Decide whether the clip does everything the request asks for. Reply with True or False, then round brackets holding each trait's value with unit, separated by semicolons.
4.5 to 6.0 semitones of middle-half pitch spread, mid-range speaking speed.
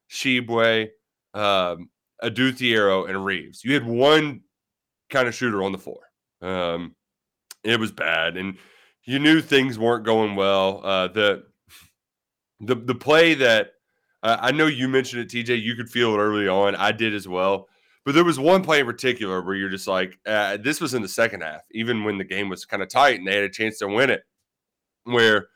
True (4.8 semitones; 195 wpm)